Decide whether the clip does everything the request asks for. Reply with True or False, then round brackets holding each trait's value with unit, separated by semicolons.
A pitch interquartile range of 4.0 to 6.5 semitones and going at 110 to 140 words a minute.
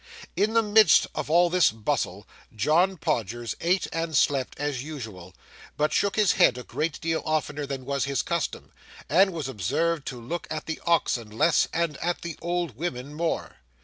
False (4.9 semitones; 180 wpm)